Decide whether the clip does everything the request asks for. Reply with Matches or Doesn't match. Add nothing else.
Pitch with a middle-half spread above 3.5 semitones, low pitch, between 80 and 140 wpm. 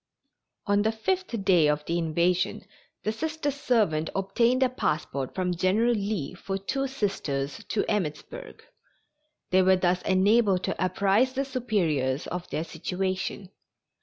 Doesn't match